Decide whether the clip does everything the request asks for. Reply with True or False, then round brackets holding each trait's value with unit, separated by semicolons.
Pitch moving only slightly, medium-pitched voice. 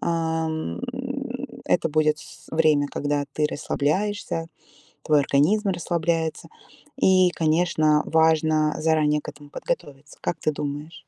True (1.7 semitones; 155 Hz)